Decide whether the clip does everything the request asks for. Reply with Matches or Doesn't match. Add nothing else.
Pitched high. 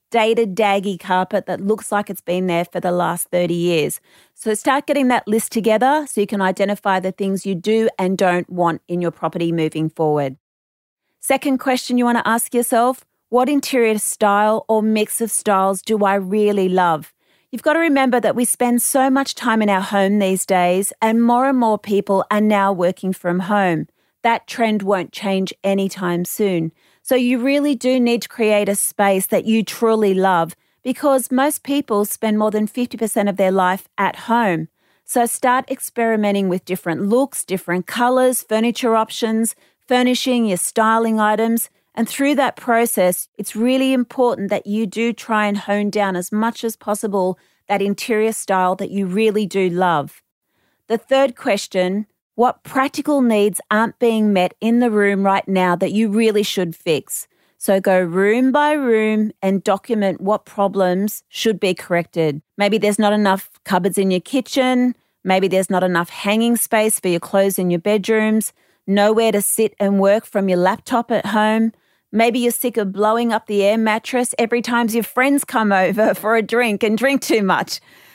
Matches